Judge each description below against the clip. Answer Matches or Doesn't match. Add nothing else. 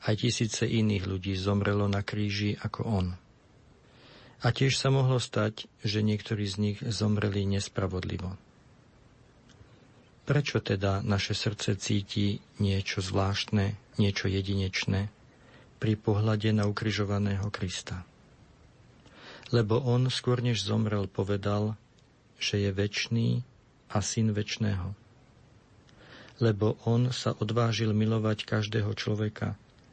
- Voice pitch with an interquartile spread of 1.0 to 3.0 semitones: Matches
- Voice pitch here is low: Matches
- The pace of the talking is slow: Matches